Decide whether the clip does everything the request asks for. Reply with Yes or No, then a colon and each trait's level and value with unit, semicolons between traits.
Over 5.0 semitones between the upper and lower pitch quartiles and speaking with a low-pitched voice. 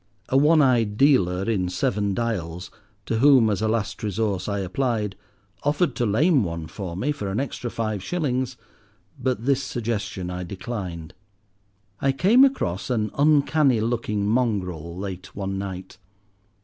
Yes: wide, 5.4 semitones; low, 110 Hz